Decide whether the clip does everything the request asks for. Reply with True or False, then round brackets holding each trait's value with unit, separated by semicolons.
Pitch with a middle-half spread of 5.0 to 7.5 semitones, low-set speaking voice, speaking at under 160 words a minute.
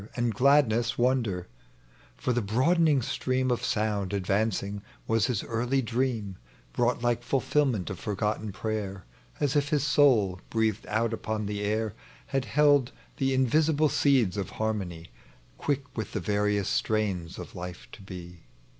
False (4.3 semitones; 110 Hz; 145 wpm)